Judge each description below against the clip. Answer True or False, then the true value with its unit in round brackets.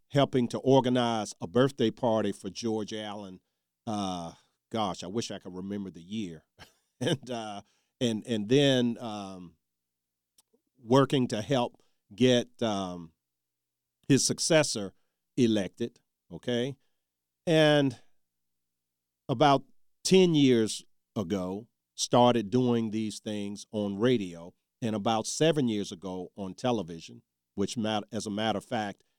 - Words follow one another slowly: True (120 wpm)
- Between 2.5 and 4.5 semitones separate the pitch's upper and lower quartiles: False (5.2 semitones)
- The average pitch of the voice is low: True (105 Hz)